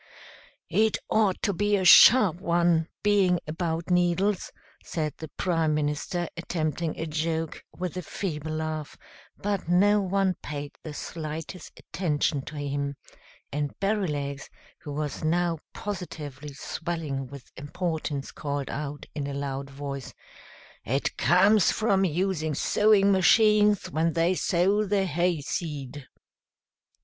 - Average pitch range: Yes, average, 4.2 semitones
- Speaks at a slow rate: Yes, slow, 125 wpm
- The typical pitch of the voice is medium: Yes, medium, 165 Hz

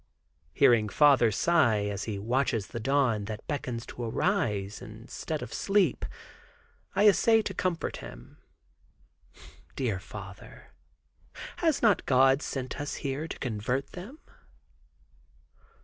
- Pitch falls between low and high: No, low, 125 Hz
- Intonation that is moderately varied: No, wide, 6.6 semitones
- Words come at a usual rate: No, slow, 115 wpm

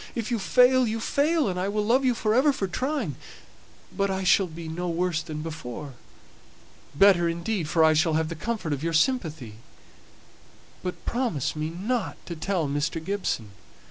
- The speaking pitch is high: No, medium, 180 Hz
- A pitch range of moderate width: No, wide, 6.0 semitones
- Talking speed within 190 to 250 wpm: No, average, 180 wpm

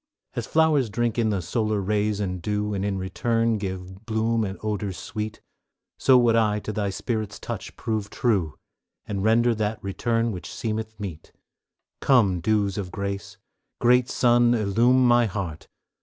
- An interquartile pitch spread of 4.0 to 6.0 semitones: No, average, 2.8 semitones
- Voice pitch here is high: No, low, 105 Hz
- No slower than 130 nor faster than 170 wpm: Yes, average, 155 wpm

